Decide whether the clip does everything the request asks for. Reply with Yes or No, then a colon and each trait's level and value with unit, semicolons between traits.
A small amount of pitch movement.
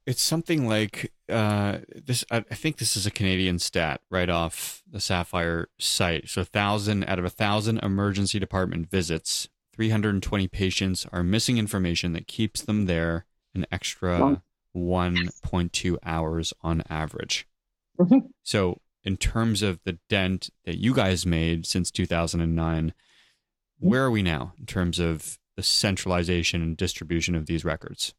No: average, 3.7 semitones